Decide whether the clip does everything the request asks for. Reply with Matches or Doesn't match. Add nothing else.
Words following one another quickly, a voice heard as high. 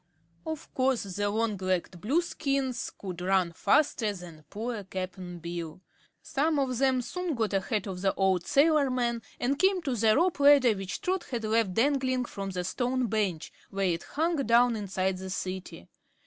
Doesn't match